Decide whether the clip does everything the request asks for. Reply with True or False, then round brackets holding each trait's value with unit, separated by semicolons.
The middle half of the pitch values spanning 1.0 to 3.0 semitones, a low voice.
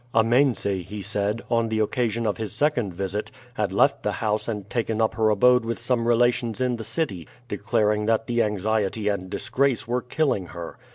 True (2.5 semitones; 110 Hz)